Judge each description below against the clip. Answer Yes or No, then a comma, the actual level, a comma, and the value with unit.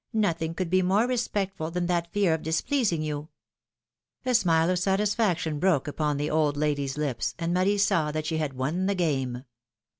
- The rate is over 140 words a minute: Yes, average, 185 wpm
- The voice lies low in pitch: No, medium, 165 Hz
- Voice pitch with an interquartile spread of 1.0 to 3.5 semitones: No, average, 4.1 semitones